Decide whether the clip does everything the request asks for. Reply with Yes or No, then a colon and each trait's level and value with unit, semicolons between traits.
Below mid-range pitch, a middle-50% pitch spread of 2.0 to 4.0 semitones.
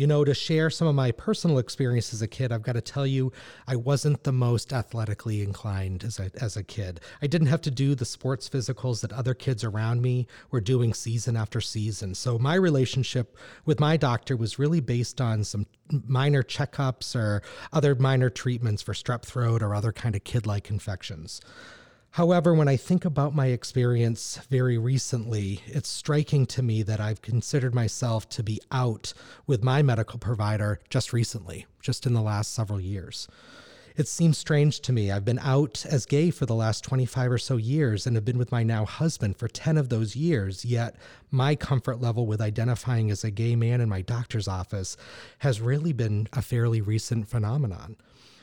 Yes: low, 120 Hz; average, 3.6 semitones